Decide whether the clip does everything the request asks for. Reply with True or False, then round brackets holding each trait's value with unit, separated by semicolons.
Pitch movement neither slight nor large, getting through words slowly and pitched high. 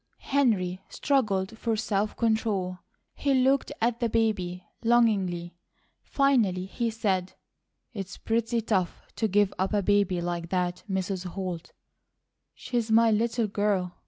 True (3.8 semitones; 130 wpm; 205 Hz)